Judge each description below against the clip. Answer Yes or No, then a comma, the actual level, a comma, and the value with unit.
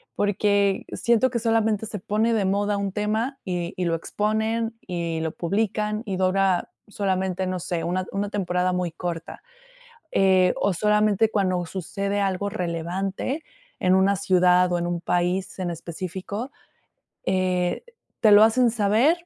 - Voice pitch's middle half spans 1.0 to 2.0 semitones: No, average, 2.7 semitones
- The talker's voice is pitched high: Yes, high, 195 Hz